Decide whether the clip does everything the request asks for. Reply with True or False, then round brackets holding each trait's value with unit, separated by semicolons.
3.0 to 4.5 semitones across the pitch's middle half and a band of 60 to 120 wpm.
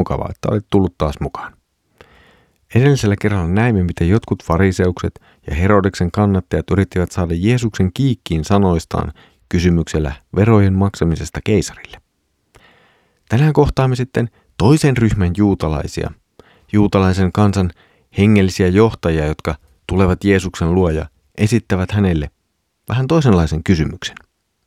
True (3.9 semitones; 105 wpm)